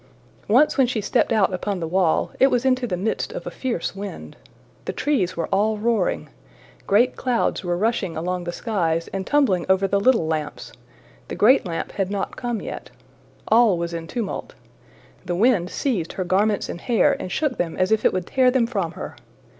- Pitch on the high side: Yes, high, 200 Hz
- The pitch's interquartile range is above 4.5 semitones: Yes, average, 5.2 semitones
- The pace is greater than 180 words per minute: Yes, average, 195 wpm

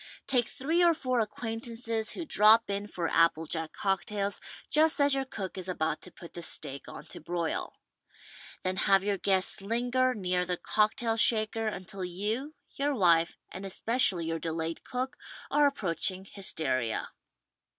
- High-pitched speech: Yes, high, 200 Hz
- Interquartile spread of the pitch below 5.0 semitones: No, average, 5.3 semitones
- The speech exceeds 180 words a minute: No, average, 160 wpm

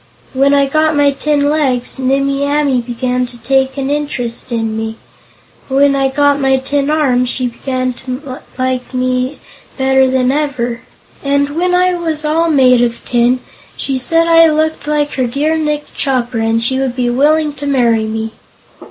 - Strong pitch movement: No, average, 2.7 semitones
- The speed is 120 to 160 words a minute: No, average, 170 wpm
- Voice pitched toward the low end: No, very high, 270 Hz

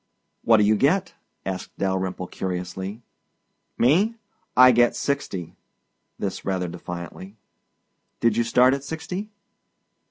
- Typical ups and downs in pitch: No, wide, 6.6 semitones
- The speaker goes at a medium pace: No, slow, 115 wpm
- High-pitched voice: No, low, 110 Hz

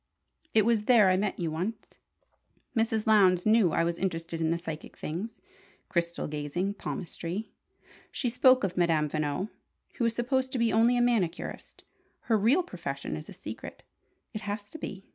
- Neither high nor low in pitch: No, high, 195 Hz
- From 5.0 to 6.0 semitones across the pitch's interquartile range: Yes, average, 5.3 semitones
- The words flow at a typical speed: Yes, average, 170 wpm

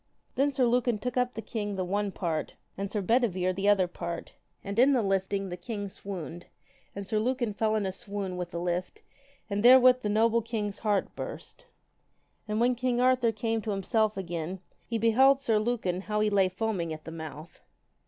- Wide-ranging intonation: No, average, 3.9 semitones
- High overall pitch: Yes, high, 210 Hz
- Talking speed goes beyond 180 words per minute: Yes, average, 195 wpm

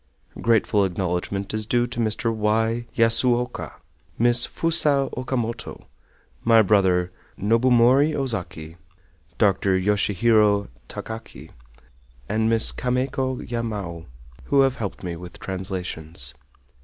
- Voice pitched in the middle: No, low, 110 Hz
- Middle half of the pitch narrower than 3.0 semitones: No, average, 4.0 semitones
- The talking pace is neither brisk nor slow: No, slow, 100 wpm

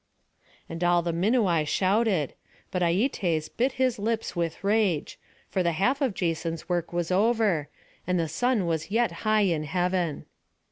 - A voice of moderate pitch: Yes, medium, 180 Hz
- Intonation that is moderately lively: Yes, average, 4.5 semitones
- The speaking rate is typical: Yes, average, 155 wpm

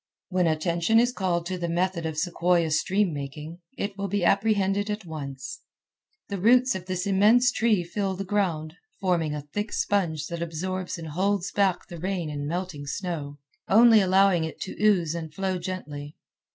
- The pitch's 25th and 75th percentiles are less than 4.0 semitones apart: Yes, average, 3.5 semitones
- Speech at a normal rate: Yes, average, 175 wpm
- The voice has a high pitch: No, medium, 180 Hz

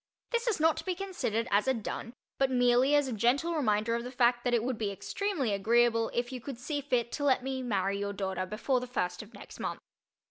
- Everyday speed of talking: No, fast, 240 wpm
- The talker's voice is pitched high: Yes, high, 245 Hz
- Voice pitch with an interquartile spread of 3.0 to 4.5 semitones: Yes, average, 3.7 semitones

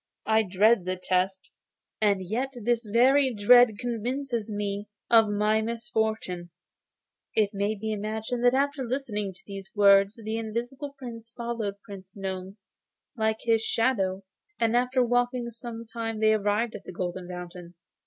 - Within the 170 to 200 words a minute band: No, average, 145 wpm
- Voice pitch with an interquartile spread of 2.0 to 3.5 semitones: Yes, average, 3.1 semitones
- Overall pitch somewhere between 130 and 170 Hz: No, high, 220 Hz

